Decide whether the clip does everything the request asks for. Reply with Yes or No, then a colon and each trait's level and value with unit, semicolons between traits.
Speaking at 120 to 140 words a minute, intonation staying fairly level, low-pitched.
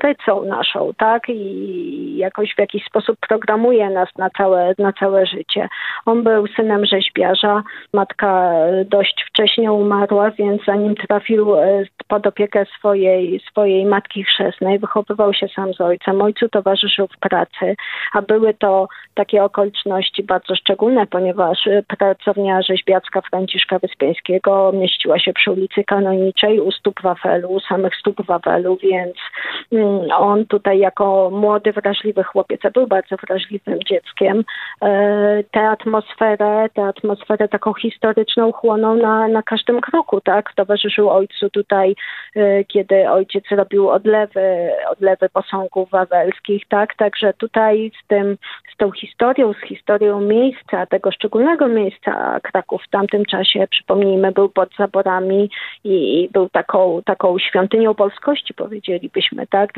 No: average, 130 wpm; narrow, 1.9 semitones; high, 205 Hz